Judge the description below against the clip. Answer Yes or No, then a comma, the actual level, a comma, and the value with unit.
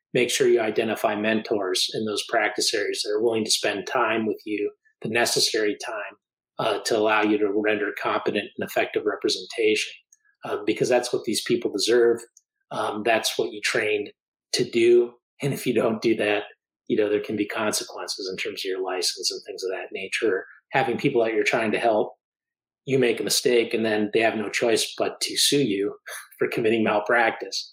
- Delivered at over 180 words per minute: Yes, average, 195 wpm